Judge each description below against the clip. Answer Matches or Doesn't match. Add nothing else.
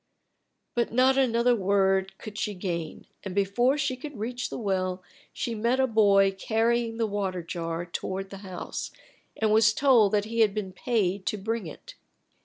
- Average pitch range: Matches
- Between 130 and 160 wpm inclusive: Doesn't match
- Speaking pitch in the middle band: Doesn't match